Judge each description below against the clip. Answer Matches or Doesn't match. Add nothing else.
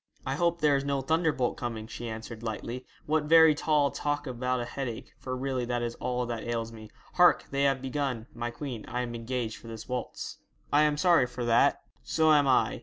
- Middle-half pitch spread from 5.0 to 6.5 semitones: Doesn't match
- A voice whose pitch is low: Matches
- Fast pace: Matches